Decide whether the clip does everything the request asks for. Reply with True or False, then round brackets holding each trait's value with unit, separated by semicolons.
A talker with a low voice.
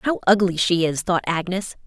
False (185 Hz)